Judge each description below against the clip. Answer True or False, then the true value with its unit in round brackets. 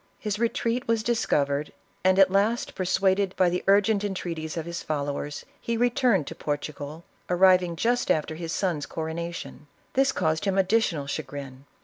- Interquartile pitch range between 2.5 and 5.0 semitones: True (4.7 semitones)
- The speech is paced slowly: False (155 wpm)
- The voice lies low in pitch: False (180 Hz)